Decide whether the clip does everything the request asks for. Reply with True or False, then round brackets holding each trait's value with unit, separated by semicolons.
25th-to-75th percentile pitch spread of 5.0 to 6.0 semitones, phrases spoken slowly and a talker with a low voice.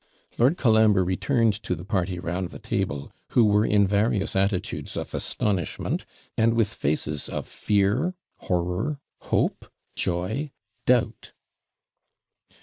False (4.0 semitones; 120 wpm; 100 Hz)